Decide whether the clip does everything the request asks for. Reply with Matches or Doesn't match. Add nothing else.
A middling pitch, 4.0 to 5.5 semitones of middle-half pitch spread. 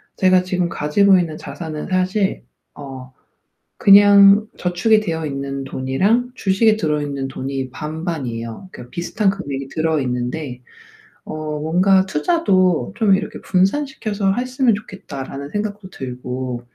Doesn't match